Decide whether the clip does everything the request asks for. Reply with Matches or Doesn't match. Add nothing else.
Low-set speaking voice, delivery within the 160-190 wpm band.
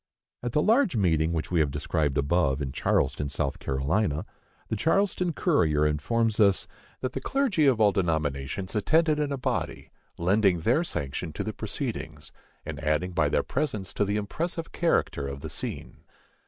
Matches